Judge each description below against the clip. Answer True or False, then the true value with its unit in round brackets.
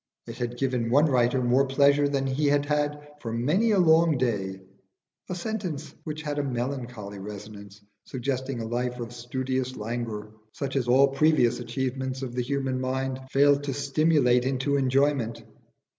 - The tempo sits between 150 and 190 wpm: True (160 wpm)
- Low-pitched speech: True (130 Hz)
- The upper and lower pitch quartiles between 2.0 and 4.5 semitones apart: True (2.8 semitones)